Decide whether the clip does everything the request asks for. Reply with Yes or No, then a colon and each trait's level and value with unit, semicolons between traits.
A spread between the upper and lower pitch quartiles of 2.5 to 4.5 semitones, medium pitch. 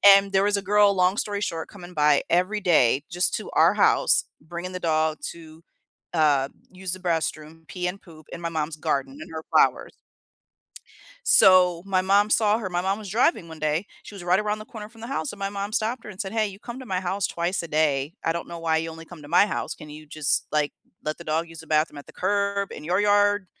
Yes: average, 4.2 semitones; medium, 180 Hz